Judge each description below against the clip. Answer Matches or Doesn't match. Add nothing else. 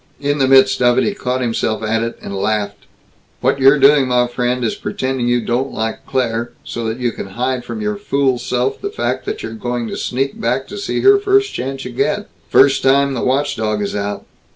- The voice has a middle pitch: Doesn't match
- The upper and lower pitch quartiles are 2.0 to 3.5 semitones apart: Matches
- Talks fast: Matches